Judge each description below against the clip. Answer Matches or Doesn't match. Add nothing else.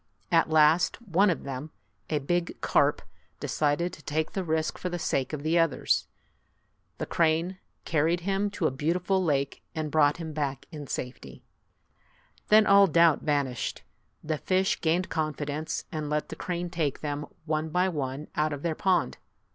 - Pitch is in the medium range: Matches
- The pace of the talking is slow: Doesn't match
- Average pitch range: Matches